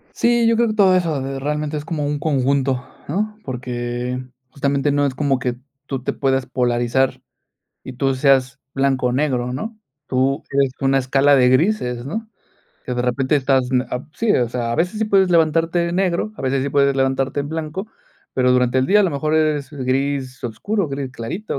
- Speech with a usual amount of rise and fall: Yes, average, 3.5 semitones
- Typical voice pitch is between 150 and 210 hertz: No, medium, 140 Hz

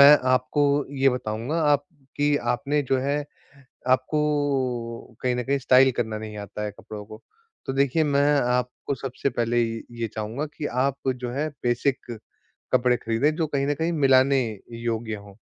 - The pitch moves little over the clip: No, average, 3.3 semitones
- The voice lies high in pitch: No, low, 130 Hz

